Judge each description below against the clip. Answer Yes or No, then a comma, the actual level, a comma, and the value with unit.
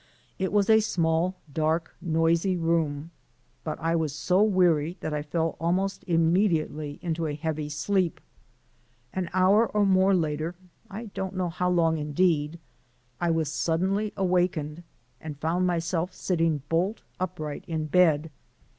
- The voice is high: No, medium, 170 Hz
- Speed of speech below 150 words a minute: Yes, average, 140 wpm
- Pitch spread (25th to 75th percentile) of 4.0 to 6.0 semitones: No, average, 2.8 semitones